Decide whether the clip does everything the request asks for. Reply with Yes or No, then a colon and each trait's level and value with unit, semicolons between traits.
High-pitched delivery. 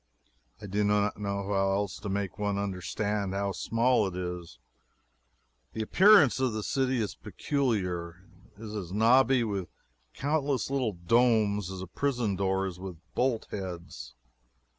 No: low, 100 Hz